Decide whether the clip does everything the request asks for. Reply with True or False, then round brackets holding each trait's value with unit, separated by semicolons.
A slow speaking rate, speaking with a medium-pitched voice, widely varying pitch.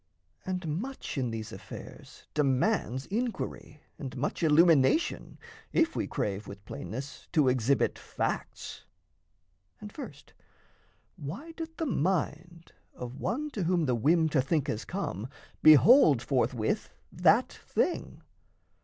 True (120 wpm; 150 Hz; 6.9 semitones)